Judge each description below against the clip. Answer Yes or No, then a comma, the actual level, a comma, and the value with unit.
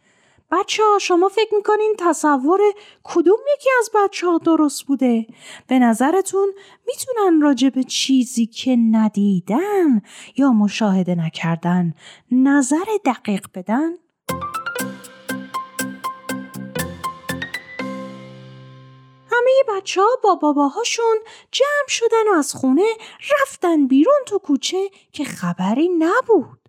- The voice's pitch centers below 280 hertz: No, very high, 295 Hz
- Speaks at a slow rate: Yes, slow, 95 wpm